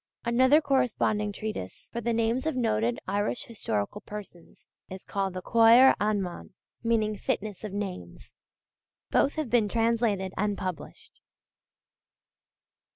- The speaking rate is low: Yes, slow, 120 wpm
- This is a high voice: Yes, high, 215 Hz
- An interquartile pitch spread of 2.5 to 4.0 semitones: Yes, average, 3.3 semitones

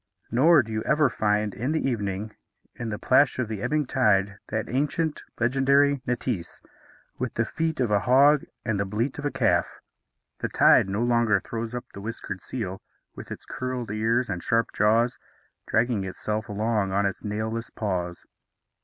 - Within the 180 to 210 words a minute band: No, average, 170 wpm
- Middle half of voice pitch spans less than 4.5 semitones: Yes, average, 3.7 semitones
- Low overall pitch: Yes, low, 115 Hz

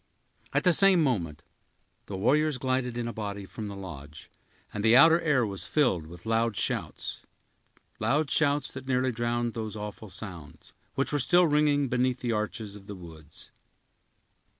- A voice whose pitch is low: Yes, low, 115 Hz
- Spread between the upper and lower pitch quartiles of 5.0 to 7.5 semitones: Yes, wide, 5.4 semitones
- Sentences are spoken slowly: No, average, 155 wpm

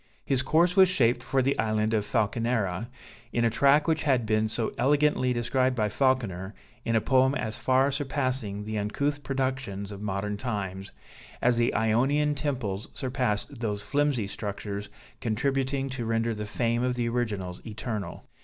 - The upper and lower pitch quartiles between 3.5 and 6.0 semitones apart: Yes, average, 4.1 semitones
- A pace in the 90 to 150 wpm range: No, average, 160 wpm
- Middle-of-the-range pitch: No, low, 120 Hz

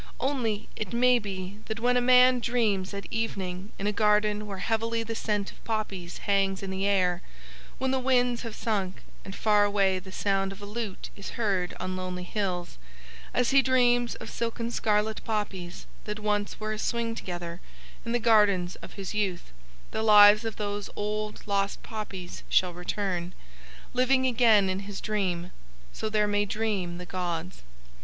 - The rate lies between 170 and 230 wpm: Yes, average, 175 wpm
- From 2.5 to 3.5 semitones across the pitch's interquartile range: Yes, average, 3.0 semitones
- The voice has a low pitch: No, high, 210 Hz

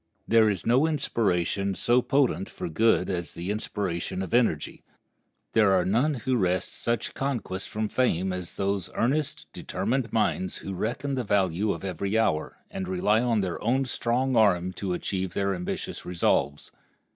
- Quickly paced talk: No, average, 160 wpm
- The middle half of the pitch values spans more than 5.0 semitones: No, average, 4.5 semitones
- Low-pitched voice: Yes, low, 100 Hz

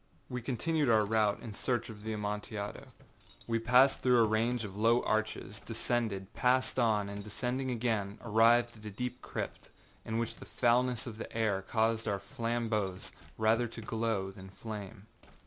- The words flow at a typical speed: Yes, average, 165 wpm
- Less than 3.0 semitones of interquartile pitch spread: Yes, narrow, 2.4 semitones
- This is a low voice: Yes, low, 110 Hz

